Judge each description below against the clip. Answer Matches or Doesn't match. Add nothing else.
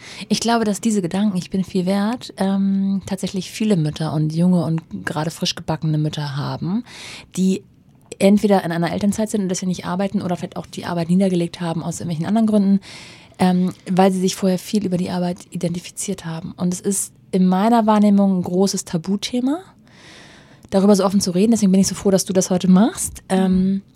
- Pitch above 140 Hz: Matches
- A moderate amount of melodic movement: Doesn't match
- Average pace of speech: Doesn't match